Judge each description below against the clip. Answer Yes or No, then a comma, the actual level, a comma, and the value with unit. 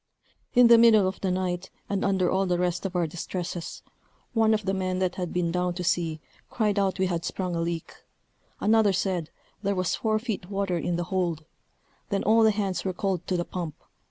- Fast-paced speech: Yes, fast, 210 wpm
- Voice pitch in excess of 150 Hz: Yes, medium, 185 Hz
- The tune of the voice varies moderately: No, narrow, 2.2 semitones